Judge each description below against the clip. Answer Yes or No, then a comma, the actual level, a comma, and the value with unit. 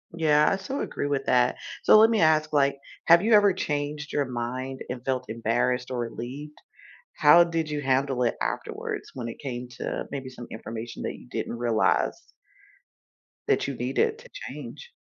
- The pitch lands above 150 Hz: No, low, 135 Hz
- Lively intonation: No, average, 3.9 semitones